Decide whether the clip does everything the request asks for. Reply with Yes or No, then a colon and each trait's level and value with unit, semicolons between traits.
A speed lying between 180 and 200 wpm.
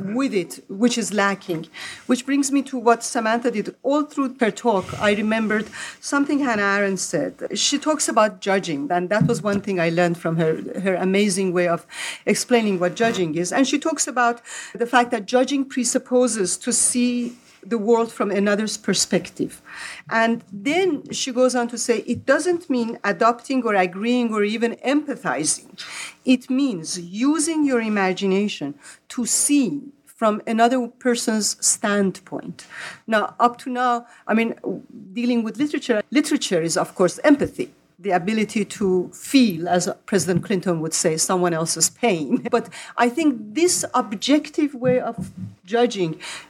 No: average, 155 wpm